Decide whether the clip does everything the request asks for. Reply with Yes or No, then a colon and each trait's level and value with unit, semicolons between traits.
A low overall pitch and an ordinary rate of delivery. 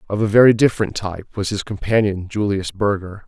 Yes: low, 100 Hz; average, 185 wpm